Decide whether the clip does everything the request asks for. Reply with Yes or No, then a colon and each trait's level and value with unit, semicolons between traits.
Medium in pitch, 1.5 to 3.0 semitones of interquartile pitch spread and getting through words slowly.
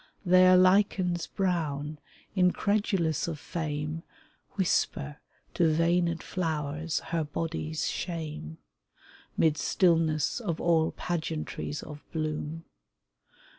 Yes: medium, 165 Hz; narrow, 2.6 semitones; slow, 90 wpm